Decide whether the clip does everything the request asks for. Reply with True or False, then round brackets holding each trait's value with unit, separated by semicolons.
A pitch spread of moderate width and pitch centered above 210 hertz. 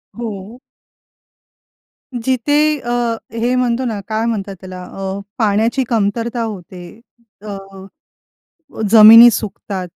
True (3.2 semitones; 225 Hz)